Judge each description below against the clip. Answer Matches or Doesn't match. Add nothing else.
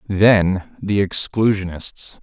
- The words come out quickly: Doesn't match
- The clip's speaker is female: Doesn't match